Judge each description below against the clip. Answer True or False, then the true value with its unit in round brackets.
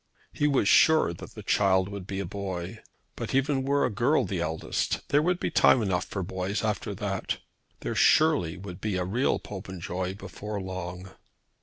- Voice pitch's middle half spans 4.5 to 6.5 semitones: True (5.5 semitones)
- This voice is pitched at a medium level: False (100 Hz)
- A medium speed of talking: True (180 wpm)